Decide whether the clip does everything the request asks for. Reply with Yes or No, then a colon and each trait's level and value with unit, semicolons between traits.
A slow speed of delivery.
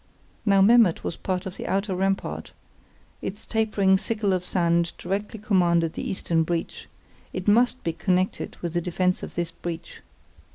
No: average, 160 wpm